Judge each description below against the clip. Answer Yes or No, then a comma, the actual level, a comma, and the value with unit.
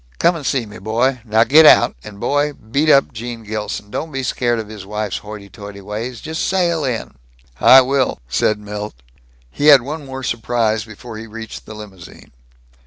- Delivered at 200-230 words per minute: No, average, 185 wpm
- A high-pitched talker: No, low, 115 Hz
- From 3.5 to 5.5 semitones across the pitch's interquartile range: Yes, average, 4.1 semitones